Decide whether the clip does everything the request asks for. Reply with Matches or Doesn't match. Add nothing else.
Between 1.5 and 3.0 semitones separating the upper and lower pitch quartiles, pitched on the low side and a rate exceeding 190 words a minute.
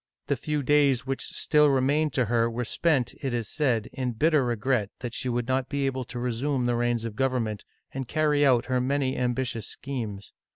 Matches